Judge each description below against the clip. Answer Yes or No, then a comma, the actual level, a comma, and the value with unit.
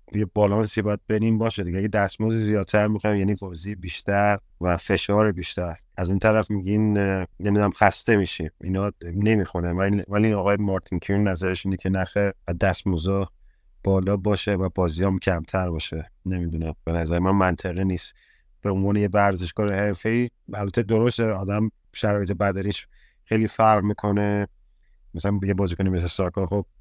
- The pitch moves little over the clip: Yes, narrow, 1.9 semitones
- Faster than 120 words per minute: Yes, average, 150 wpm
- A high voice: No, low, 100 Hz